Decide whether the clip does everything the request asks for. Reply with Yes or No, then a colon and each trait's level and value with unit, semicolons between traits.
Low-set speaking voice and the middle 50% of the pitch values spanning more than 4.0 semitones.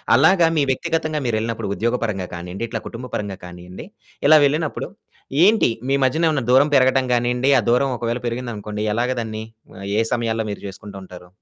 Yes: low, 120 Hz; average, 4.4 semitones